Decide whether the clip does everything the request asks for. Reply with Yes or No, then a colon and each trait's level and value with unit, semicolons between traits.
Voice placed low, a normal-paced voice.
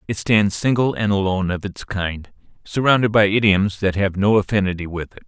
Yes: low, 100 Hz; average, 195 wpm